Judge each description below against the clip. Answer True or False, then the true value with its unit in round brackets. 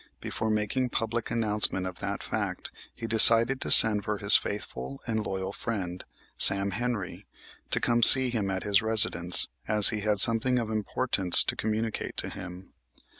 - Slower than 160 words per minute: False (170 wpm)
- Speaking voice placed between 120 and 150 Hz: False (105 Hz)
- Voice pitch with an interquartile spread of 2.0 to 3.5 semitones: True (2.6 semitones)